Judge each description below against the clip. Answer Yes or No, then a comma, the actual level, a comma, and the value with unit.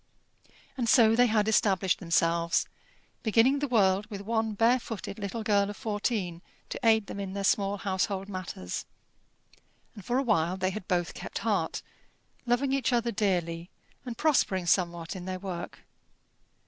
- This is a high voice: Yes, high, 200 Hz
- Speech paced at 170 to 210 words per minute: No, average, 160 wpm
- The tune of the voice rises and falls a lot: No, average, 3.5 semitones